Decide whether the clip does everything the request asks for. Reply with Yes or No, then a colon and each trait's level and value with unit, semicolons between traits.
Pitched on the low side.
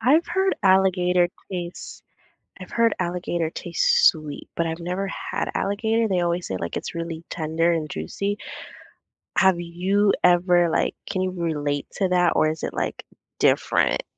No: medium, 180 Hz